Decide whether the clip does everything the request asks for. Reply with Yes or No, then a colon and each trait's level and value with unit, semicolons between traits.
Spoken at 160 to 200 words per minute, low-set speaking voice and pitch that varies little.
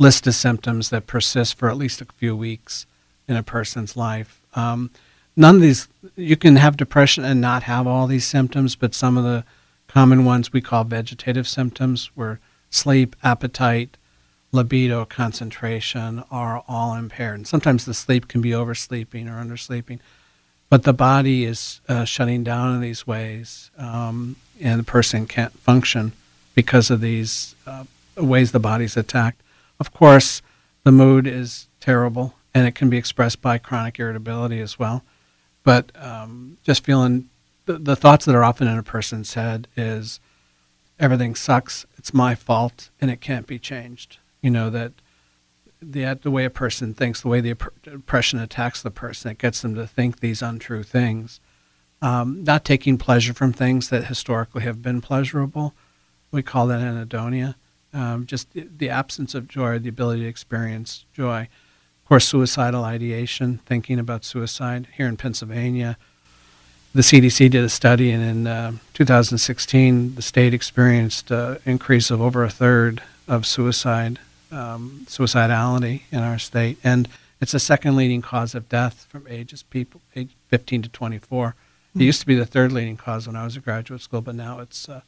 Yes: average, 170 wpm; low, 120 Hz; narrow, 2.0 semitones